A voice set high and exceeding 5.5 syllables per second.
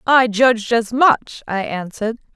No: high, 230 Hz; 4.4 syllables/s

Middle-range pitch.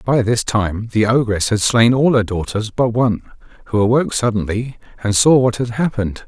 No: low, 115 Hz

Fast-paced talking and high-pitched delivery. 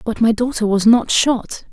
Yes: fast, 210 wpm; high, 225 Hz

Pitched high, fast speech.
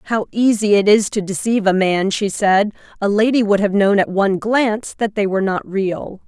Yes: high, 205 Hz; fast, 220 wpm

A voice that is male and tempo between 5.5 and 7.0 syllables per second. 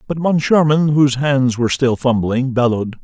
No: male; 5.3 syllables/s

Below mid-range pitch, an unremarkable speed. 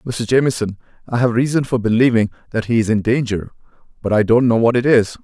No: low, 115 Hz; fast, 220 wpm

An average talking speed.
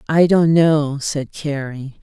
Yes: average, 150 wpm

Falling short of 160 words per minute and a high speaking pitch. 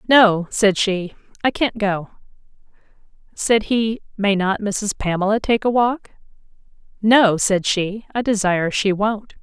Yes: slow, 135 wpm; high, 205 Hz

